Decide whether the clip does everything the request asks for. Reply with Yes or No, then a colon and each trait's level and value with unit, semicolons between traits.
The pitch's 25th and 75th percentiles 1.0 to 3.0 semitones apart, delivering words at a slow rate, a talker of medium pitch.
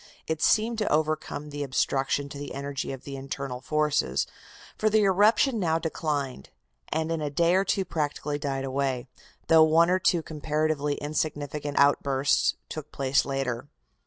No: narrow, 2.6 semitones; average, 160 wpm; medium, 150 Hz